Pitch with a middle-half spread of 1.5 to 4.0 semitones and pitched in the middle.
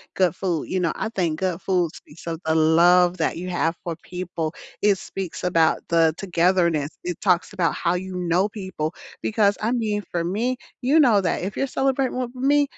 Yes: average, 3.6 semitones; medium, 180 Hz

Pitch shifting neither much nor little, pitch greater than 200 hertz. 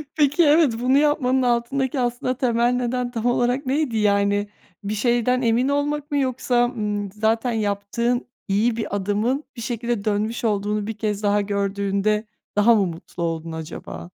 Yes: average, 3.5 semitones; high, 230 Hz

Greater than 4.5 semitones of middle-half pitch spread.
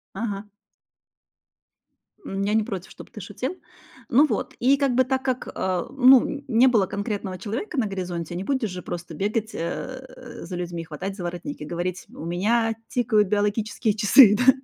Yes: average, 5.3 semitones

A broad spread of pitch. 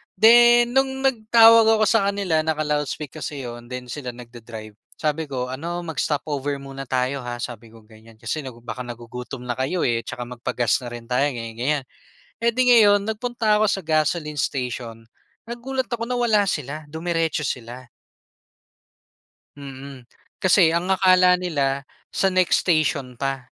Yes: wide, 7.7 semitones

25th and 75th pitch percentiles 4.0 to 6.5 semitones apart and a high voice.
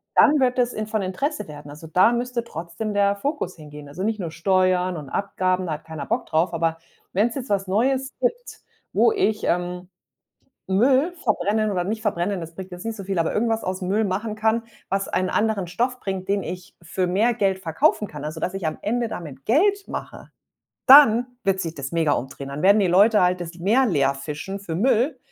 Yes: average, 4.6 semitones; high, 195 Hz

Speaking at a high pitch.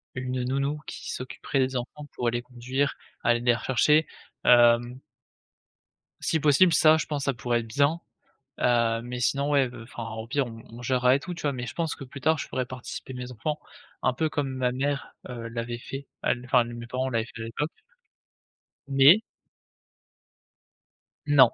No: low, 130 Hz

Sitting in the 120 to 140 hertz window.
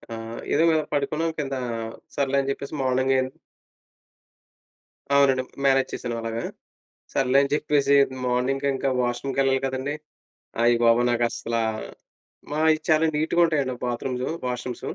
Yes: low, 135 Hz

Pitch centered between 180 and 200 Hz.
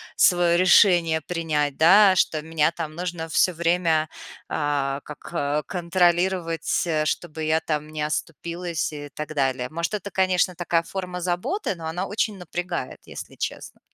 No: medium, 170 Hz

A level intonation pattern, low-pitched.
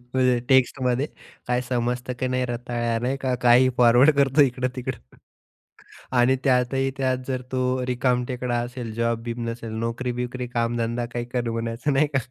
Yes: narrow, 1.3 semitones; low, 125 Hz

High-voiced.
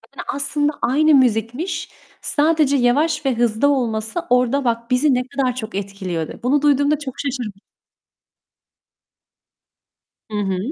Yes: very high, 255 Hz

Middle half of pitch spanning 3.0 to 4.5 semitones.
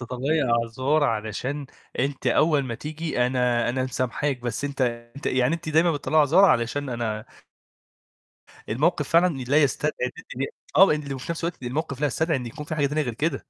Yes: average, 3.7 semitones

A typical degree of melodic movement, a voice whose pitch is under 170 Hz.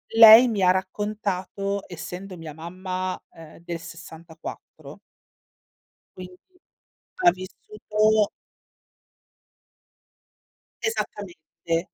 No: average, 3.6 semitones; medium, 185 Hz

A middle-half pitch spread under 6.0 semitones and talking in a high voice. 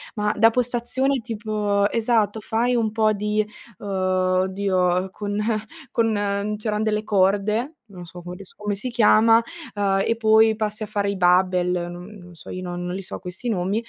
Yes: average, 2.7 semitones; high, 210 Hz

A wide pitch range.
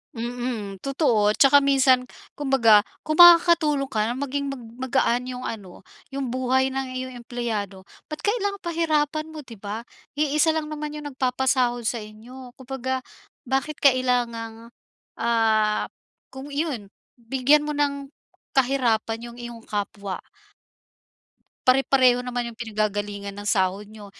No: average, 3.7 semitones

